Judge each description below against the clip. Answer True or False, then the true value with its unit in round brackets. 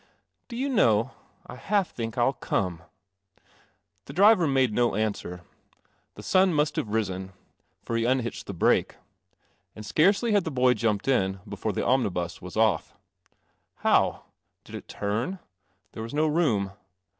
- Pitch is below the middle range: True (115 Hz)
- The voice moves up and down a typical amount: False (7.0 semitones)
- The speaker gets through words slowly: False (155 wpm)